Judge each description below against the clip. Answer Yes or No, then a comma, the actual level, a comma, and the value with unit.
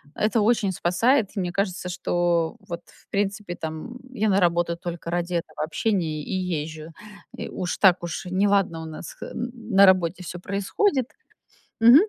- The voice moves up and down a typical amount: Yes, average, 3.1 semitones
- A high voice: No, medium, 180 Hz